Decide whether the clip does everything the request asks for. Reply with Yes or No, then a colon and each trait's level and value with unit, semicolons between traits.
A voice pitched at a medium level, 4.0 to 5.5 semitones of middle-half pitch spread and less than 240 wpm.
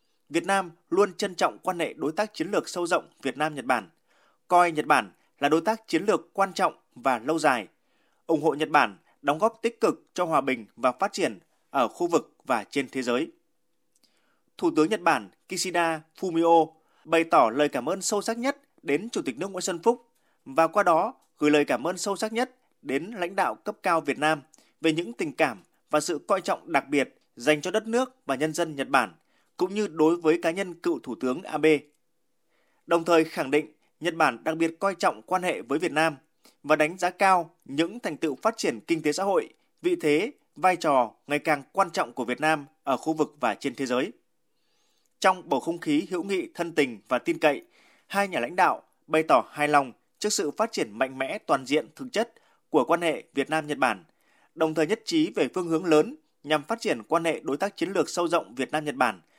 Yes: medium, 165 Hz; average, 4.3 semitones; average, 225 wpm